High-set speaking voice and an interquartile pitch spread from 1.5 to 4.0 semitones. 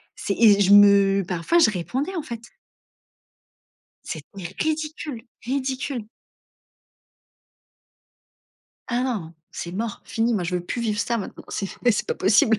No: high, 220 Hz; average, 4.5 semitones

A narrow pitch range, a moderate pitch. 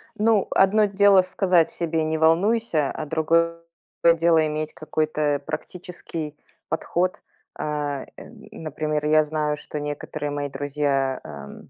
Yes: narrow, 2.3 semitones; medium, 155 Hz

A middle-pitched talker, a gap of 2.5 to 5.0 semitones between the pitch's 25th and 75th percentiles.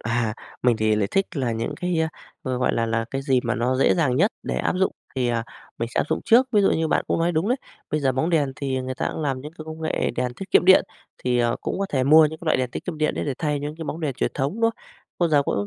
Yes: medium, 145 Hz; average, 4.4 semitones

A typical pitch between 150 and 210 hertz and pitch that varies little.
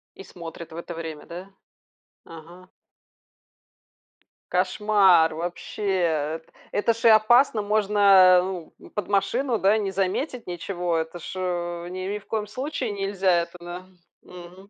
No: medium, 185 Hz; average, 3.1 semitones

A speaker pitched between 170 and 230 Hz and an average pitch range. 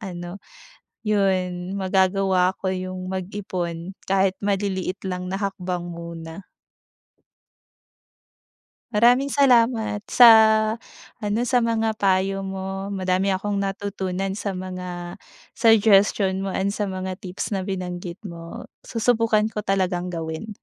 No: high, 190 Hz; narrow, 2.0 semitones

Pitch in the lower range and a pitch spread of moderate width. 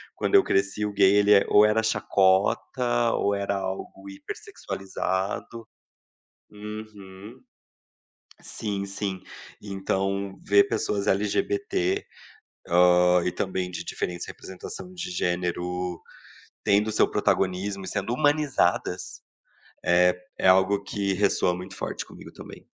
No: low, 100 Hz; narrow, 2.2 semitones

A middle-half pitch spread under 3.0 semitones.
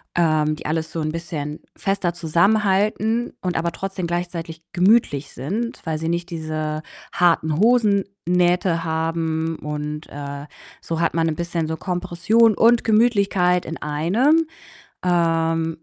No: average, 3.3 semitones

